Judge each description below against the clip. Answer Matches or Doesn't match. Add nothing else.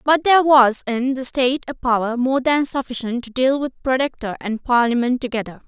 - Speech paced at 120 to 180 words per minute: Doesn't match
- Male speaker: Doesn't match